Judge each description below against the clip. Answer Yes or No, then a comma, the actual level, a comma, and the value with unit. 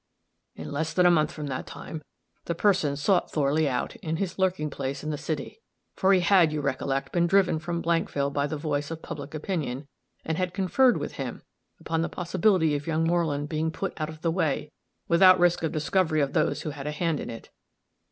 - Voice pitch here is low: No, medium, 160 Hz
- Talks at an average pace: No, fast, 215 wpm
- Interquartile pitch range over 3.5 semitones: No, average, 3.1 semitones